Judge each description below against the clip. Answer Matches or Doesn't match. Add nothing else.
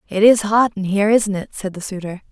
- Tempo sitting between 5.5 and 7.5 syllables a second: Matches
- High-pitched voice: Matches